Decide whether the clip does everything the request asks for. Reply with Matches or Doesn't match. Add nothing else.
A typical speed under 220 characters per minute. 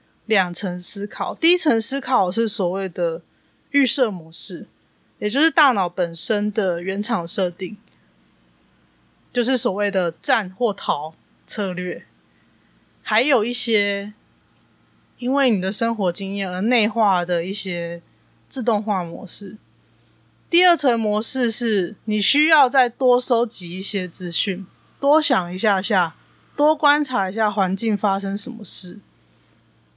Matches